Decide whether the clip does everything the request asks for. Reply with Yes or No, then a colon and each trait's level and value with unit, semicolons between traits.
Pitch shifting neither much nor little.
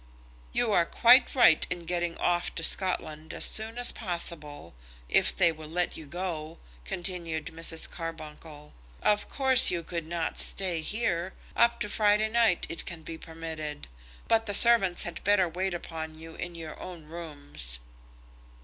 Yes: average, 3.3 semitones